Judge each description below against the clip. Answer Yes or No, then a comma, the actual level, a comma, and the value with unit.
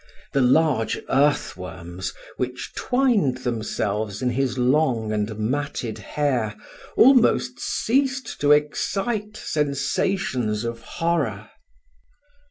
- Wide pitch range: Yes, wide, 6.3 semitones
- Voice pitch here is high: No, low, 130 Hz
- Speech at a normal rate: No, slow, 95 wpm